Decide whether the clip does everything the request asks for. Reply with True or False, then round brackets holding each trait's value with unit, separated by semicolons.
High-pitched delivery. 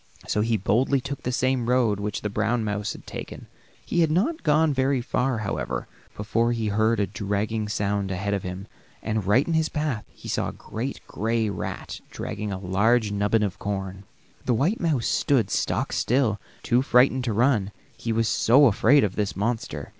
False (115 Hz)